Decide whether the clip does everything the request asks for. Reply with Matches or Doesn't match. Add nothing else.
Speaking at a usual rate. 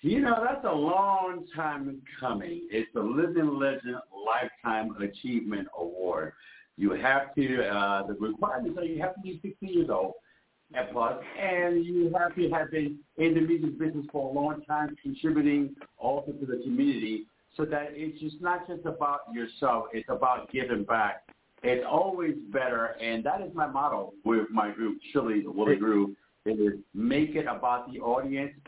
Matches